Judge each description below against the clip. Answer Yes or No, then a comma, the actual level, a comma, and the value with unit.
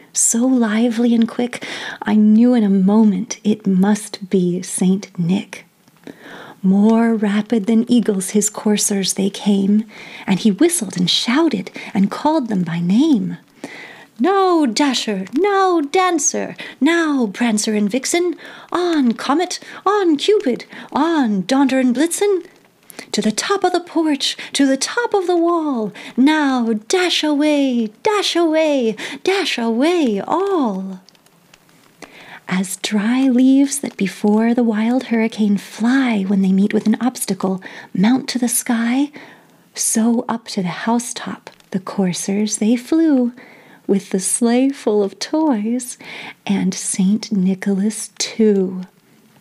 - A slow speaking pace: Yes, slow, 130 wpm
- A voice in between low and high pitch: No, high, 235 Hz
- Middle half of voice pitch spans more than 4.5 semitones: Yes, wide, 5.6 semitones